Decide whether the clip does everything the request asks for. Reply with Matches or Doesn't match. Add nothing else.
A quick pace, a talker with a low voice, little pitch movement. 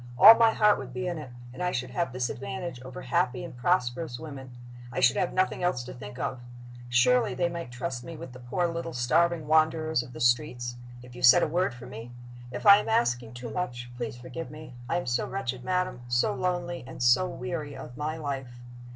Doesn't match